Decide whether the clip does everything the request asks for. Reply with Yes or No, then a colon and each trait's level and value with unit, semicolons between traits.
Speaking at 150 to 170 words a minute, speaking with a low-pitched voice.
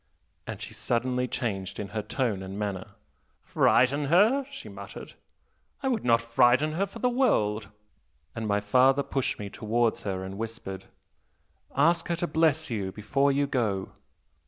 Yes: average, 155 wpm; low, 120 Hz